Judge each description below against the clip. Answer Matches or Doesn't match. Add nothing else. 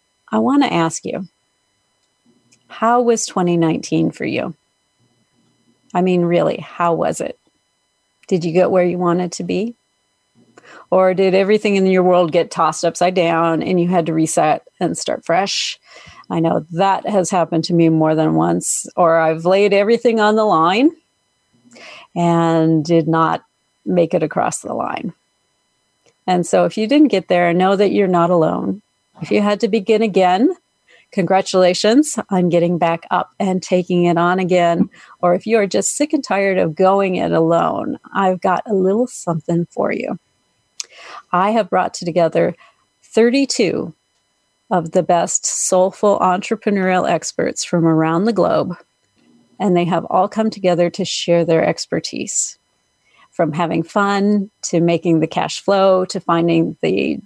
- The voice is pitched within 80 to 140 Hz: Doesn't match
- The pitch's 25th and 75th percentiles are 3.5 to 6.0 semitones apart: Doesn't match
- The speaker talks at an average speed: Matches